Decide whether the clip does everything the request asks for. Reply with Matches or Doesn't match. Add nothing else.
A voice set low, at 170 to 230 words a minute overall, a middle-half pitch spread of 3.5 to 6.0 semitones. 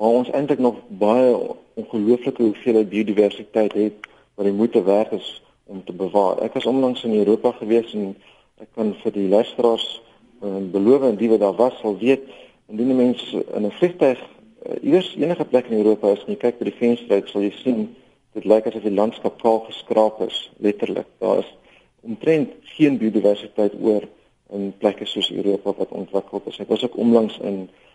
Doesn't match